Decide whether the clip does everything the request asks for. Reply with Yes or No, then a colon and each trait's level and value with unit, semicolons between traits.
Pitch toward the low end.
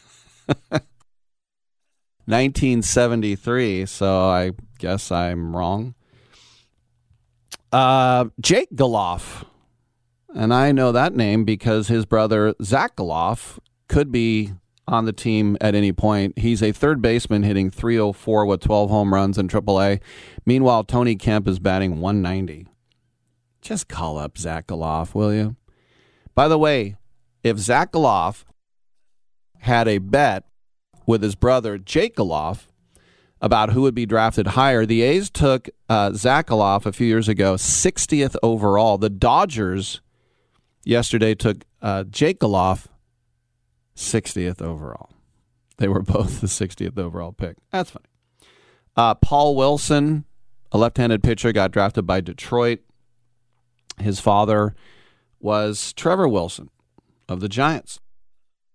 Yes: low, 110 Hz